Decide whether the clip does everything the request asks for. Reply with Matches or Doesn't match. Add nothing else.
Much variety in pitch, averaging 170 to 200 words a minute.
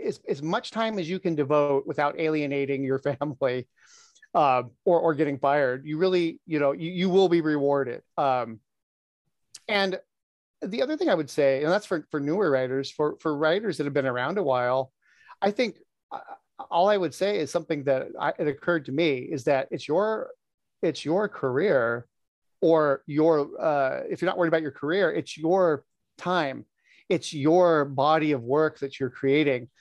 Doesn't match